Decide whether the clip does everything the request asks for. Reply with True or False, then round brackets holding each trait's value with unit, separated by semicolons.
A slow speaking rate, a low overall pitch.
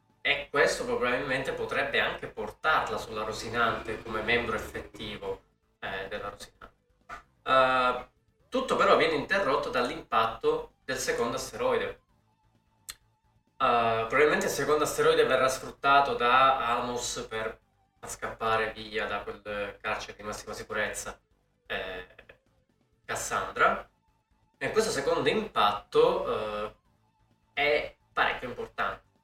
True (105 wpm; 125 Hz)